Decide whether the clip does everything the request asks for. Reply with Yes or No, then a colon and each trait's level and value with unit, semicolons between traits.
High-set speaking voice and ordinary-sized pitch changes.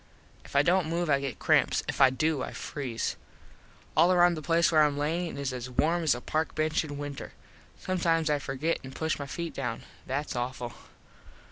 No: medium, 150 Hz; average, 3.4 semitones